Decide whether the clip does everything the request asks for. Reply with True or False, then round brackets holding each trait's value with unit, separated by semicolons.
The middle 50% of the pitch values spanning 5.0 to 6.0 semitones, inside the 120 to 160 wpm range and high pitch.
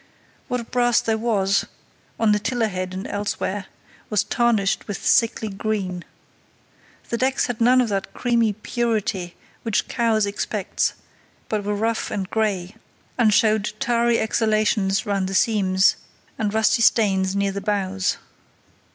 False (2.7 semitones; 140 wpm; 215 Hz)